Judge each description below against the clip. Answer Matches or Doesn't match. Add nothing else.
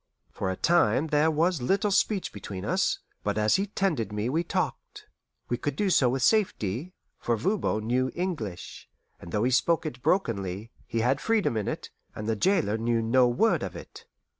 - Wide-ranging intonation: Matches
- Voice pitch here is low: Matches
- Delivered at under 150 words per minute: Doesn't match